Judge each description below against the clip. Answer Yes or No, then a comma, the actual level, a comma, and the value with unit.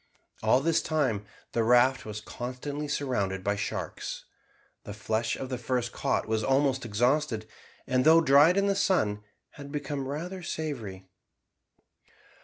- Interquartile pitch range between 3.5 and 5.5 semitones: Yes, average, 5.1 semitones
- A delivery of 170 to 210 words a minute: No, average, 140 wpm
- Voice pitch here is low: Yes, low, 130 Hz